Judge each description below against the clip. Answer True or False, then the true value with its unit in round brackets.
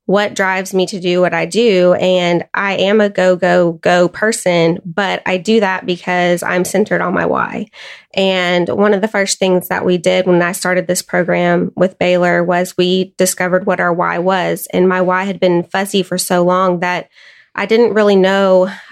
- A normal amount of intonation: False (1.3 semitones)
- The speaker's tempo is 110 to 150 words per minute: False (200 wpm)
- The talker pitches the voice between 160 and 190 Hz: True (185 Hz)